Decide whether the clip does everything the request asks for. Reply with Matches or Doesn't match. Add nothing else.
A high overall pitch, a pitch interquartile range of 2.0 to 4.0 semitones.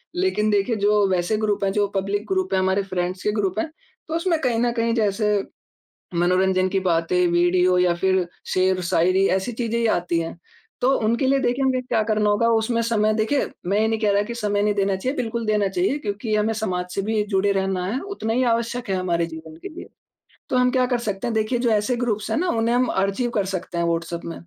Matches